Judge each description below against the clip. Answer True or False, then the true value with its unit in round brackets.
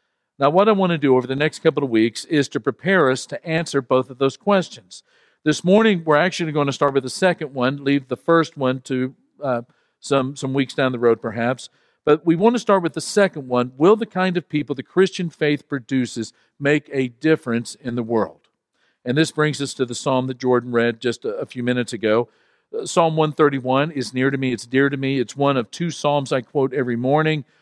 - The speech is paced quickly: True (230 wpm)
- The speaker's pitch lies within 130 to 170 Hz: True (140 Hz)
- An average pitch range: True (3.7 semitones)